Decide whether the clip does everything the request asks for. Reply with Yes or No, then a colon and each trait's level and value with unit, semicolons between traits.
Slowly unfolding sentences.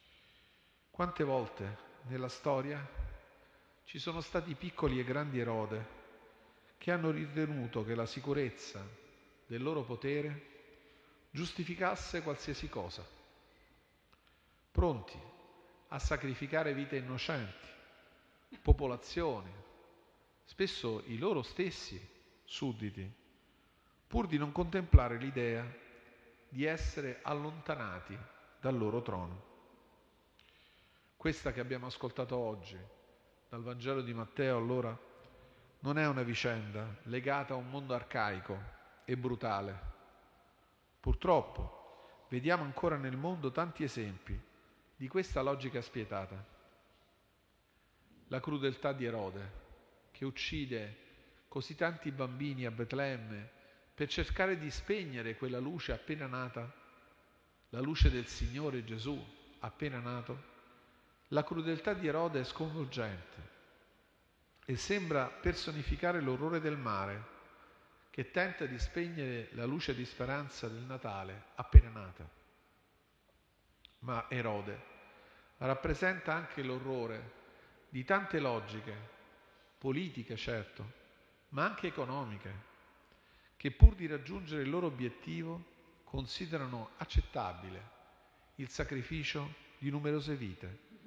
Yes: slow, 100 wpm